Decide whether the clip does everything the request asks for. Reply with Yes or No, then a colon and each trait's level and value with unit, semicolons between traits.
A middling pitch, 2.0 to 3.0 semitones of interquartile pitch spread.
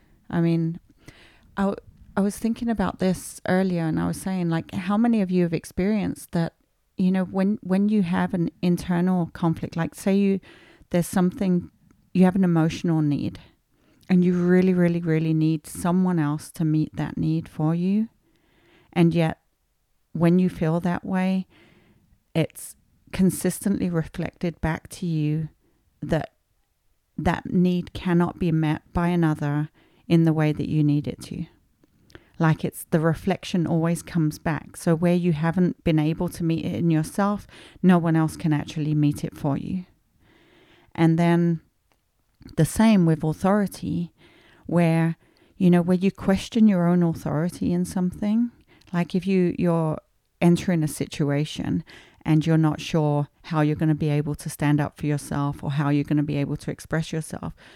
Yes: medium, 170 Hz; average, 2.7 semitones